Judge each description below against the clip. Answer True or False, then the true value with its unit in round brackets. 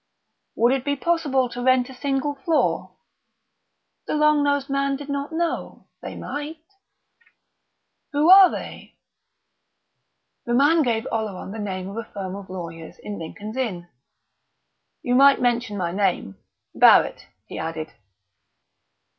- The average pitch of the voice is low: False (250 Hz)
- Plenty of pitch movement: True (6.1 semitones)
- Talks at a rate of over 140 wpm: False (135 wpm)